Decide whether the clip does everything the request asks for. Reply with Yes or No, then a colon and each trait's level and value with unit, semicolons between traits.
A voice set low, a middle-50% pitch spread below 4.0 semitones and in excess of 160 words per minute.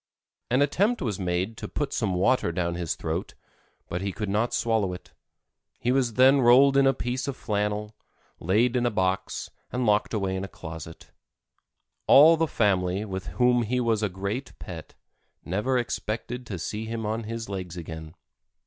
No: low, 110 Hz; average, 4.7 semitones; average, 175 wpm